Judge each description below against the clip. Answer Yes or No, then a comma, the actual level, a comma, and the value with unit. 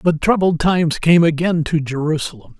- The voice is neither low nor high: Yes, medium, 160 Hz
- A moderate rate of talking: Yes, average, 160 wpm